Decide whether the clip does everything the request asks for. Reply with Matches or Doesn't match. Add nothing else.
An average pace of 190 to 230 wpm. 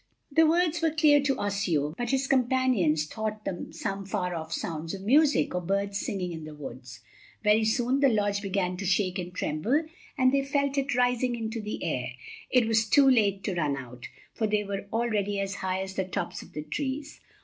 Matches